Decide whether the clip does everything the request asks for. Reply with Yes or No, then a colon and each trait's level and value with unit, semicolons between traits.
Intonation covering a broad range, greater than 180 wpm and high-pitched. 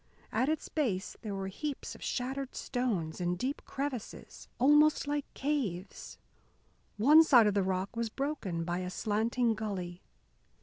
No: wide, 6.5 semitones; average, 145 wpm; high, 230 Hz